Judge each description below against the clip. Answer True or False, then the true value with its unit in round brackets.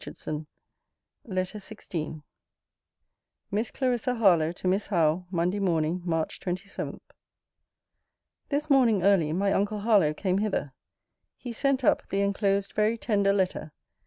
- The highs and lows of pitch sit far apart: False (3.7 semitones)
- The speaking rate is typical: False (125 wpm)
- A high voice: True (195 Hz)